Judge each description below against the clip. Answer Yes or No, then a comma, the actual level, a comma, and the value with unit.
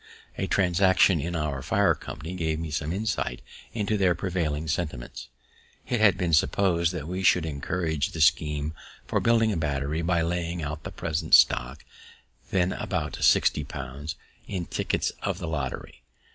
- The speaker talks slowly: No, average, 160 wpm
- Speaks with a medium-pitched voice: No, very low, 80 Hz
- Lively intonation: No, average, 3.2 semitones